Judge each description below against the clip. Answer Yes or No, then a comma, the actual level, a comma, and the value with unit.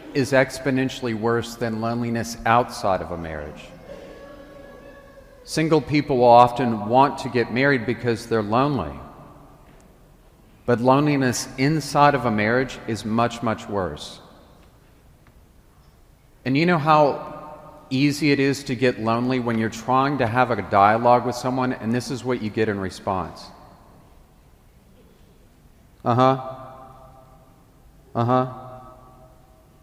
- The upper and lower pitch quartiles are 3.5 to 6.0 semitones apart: No, average, 2.8 semitones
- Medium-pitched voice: No, low, 125 Hz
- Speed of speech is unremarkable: No, slow, 120 wpm